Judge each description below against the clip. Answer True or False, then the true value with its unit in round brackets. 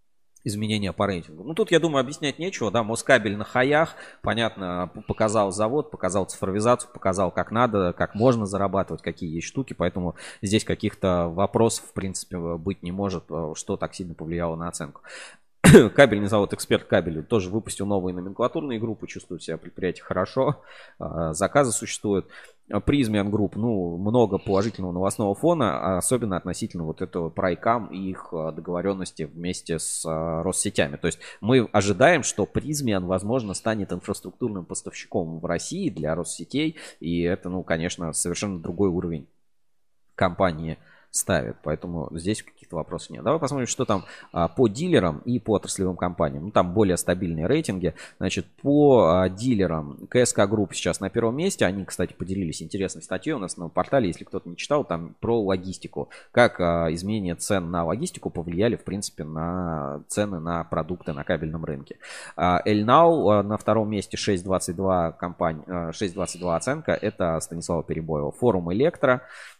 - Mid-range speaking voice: False (95 Hz)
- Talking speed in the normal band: True (150 wpm)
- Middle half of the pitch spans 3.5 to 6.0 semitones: True (3.9 semitones)